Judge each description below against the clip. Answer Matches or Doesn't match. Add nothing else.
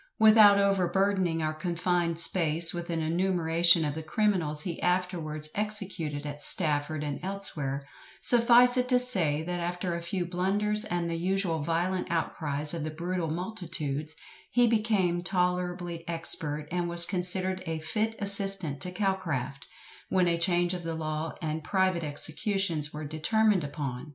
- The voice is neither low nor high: Matches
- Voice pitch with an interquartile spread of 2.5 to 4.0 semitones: Matches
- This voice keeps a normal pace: Matches